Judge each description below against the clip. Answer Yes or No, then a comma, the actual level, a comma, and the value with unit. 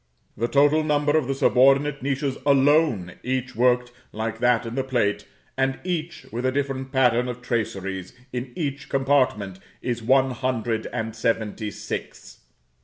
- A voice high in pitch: No, low, 130 Hz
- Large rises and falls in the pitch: No, average, 3.2 semitones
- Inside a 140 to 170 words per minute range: Yes, average, 150 wpm